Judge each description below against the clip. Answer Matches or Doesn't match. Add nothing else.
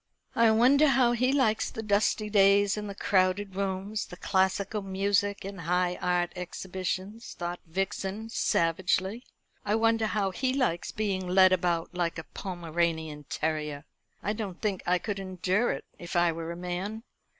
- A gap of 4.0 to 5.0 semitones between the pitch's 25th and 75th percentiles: Doesn't match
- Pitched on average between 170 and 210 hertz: Matches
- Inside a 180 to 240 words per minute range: Doesn't match